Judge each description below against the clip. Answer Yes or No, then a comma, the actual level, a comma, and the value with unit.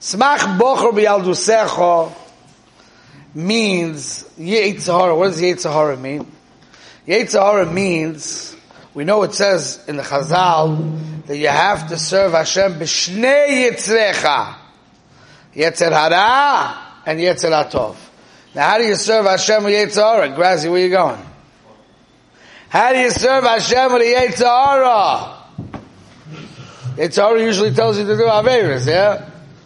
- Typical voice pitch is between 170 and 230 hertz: Yes, medium, 185 Hz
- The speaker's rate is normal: No, slow, 120 wpm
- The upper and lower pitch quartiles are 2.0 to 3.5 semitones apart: No, wide, 5.6 semitones